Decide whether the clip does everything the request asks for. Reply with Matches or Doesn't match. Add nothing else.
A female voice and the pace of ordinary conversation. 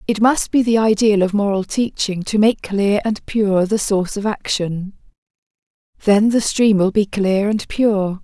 Matches